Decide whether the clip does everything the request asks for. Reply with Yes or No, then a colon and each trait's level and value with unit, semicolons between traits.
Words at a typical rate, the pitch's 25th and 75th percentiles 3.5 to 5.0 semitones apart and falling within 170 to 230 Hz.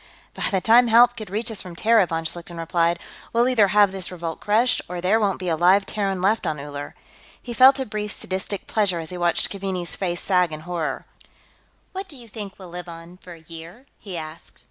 No: fast, 220 wpm; average, 4.0 semitones; medium, 185 Hz